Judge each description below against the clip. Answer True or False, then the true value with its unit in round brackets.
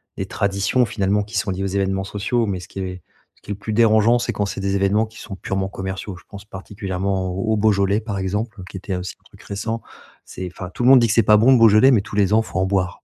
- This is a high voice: False (100 Hz)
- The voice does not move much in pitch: True (2.2 semitones)